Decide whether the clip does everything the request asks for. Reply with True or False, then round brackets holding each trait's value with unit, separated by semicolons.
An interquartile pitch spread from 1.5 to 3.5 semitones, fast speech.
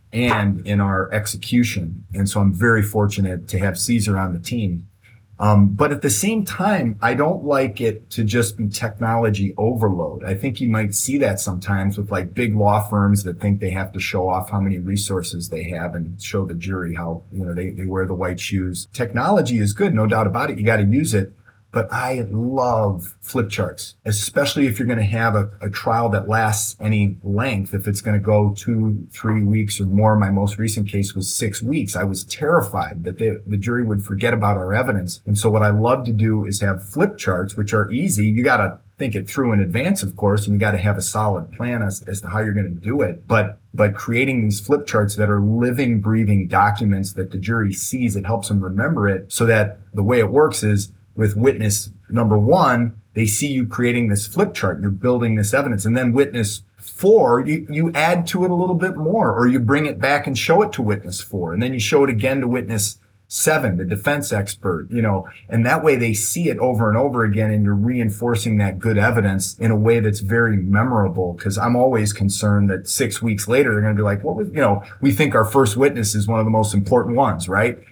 True (3.0 semitones; 230 wpm)